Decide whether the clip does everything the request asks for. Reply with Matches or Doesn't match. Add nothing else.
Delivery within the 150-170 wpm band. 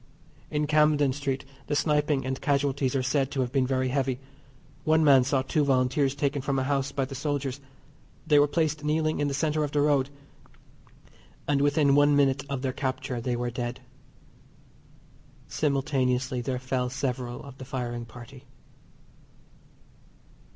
Matches